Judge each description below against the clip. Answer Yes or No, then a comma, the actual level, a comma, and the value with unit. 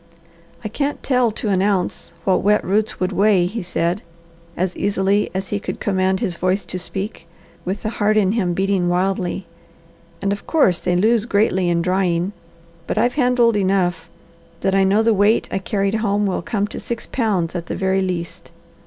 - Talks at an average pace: Yes, average, 190 wpm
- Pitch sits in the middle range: No, high, 195 Hz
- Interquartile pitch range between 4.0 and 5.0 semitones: No, narrow, 2.5 semitones